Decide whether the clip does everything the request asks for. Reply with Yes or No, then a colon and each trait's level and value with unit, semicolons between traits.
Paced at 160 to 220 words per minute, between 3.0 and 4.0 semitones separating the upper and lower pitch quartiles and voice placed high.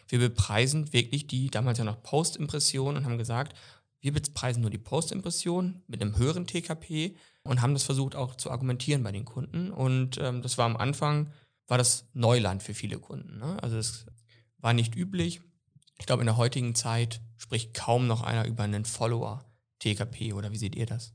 No: fast, 190 wpm; average, 3.7 semitones; low, 125 Hz